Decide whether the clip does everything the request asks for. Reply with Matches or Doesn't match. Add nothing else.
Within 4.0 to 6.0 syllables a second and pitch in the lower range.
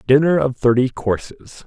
Matches